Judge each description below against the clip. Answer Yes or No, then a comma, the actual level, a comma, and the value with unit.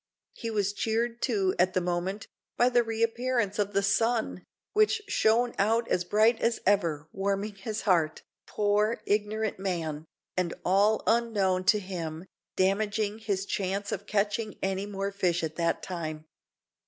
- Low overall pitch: No, high, 205 Hz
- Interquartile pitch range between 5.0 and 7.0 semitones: No, average, 2.9 semitones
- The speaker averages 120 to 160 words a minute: Yes, average, 155 wpm